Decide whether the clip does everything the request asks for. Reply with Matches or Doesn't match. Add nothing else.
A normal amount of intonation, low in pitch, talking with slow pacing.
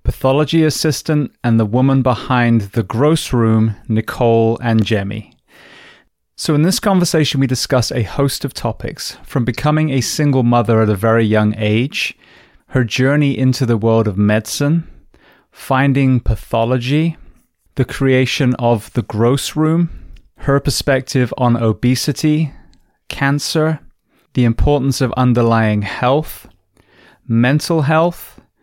Matches